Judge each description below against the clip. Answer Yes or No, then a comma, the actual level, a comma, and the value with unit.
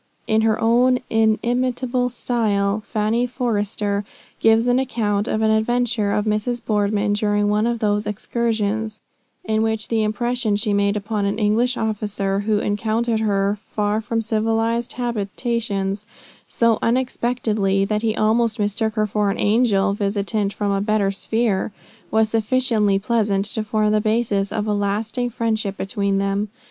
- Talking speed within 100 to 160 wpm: Yes, average, 150 wpm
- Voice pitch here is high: Yes, high, 215 Hz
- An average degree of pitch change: No, narrow, 2.0 semitones